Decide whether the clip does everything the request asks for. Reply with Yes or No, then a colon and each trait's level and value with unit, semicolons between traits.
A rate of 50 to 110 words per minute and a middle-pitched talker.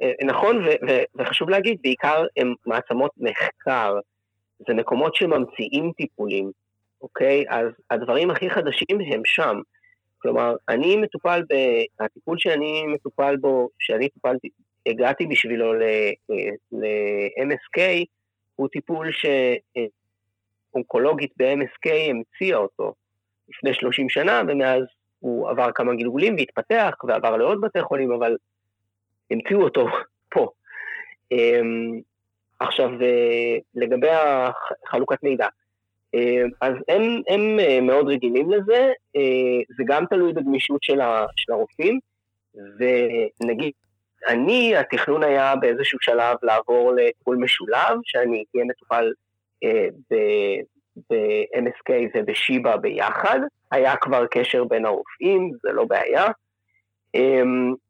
No: slow, 100 wpm; low, 130 Hz